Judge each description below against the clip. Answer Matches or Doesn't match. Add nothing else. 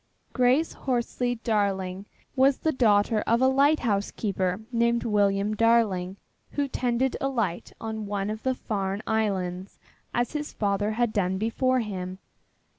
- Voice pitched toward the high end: Matches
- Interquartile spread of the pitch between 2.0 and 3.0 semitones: Doesn't match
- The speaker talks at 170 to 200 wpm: Doesn't match